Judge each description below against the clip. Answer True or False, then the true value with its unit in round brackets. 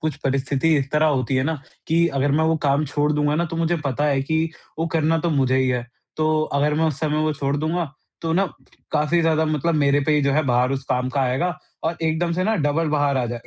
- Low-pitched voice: False (150 Hz)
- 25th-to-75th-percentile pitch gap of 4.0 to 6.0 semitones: False (2.8 semitones)